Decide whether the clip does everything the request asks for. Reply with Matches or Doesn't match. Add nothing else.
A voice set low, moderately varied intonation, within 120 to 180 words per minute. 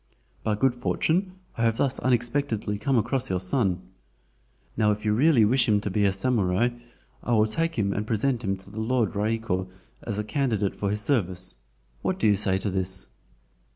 Doesn't match